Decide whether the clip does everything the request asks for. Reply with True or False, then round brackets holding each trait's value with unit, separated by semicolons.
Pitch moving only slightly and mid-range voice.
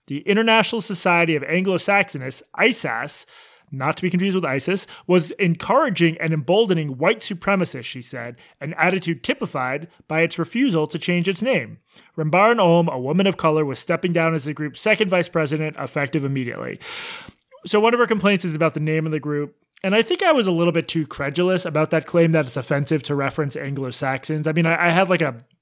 False (3.9 semitones; 165 Hz)